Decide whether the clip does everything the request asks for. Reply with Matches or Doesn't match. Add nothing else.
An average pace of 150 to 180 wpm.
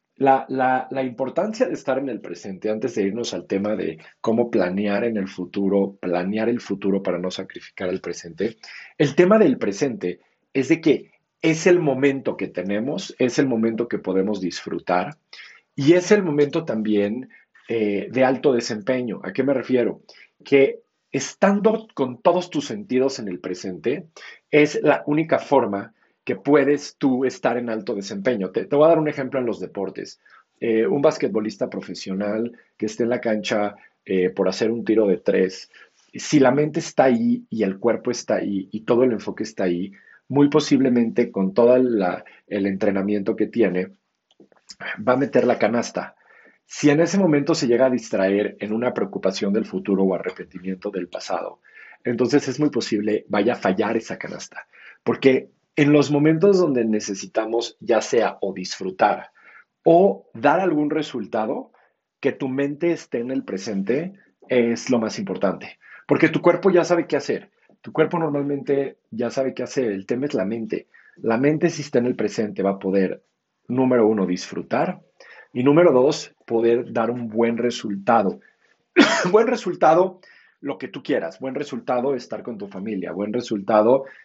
Matches